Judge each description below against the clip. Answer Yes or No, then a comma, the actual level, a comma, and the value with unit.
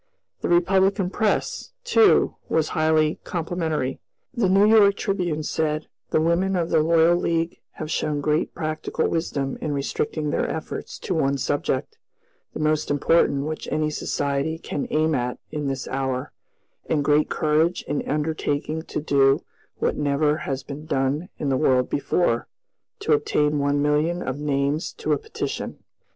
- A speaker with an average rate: Yes, average, 155 wpm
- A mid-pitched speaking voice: Yes, medium, 155 Hz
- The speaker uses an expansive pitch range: No, average, 2.7 semitones